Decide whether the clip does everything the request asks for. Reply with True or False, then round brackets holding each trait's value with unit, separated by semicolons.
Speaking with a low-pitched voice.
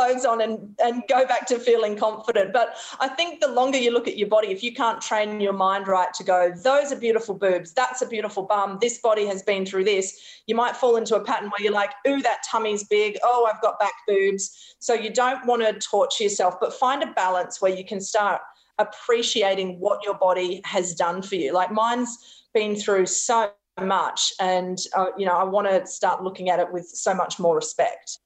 False (210 Hz)